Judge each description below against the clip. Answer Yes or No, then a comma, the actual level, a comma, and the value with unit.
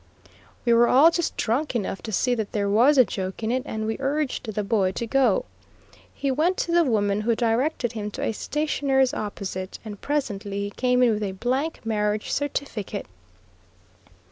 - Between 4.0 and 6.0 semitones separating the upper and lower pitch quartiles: Yes, average, 4.5 semitones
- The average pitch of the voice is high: Yes, high, 230 Hz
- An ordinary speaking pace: Yes, average, 185 wpm